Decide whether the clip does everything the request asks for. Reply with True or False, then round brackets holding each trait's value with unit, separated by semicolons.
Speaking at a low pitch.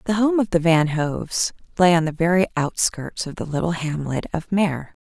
False (170 Hz)